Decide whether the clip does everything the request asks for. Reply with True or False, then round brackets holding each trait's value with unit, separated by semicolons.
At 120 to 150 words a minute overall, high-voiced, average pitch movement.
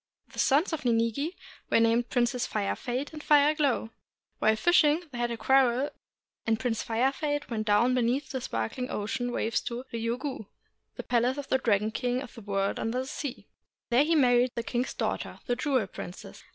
False (200 wpm; 245 Hz; 3.0 semitones)